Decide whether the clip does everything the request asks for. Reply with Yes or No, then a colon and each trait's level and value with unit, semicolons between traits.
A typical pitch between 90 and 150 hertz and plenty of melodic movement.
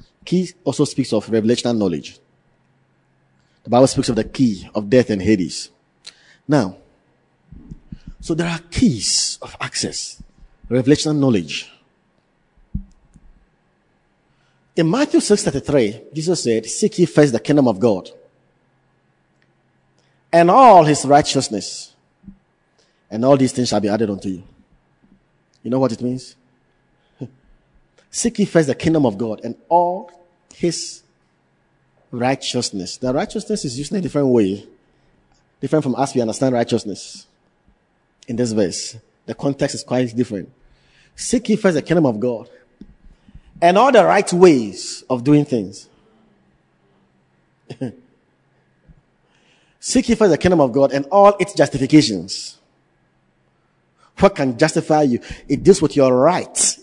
Yes: low, 135 Hz; wide, 6.8 semitones